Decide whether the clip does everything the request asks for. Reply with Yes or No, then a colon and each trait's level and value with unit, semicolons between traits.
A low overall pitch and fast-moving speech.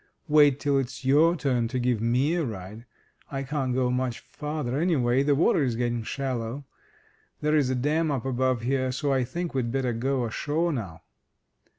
No: low, 130 Hz; average, 180 wpm